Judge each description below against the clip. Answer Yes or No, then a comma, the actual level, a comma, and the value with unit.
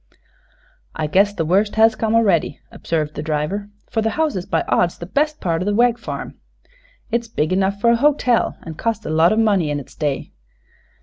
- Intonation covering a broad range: Yes, wide, 5.7 semitones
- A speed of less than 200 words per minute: No, fast, 205 wpm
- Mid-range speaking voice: No, high, 200 Hz